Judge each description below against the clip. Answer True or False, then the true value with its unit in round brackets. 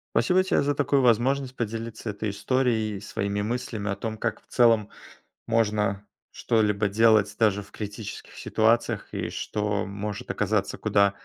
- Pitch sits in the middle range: False (110 Hz)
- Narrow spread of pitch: True (2.3 semitones)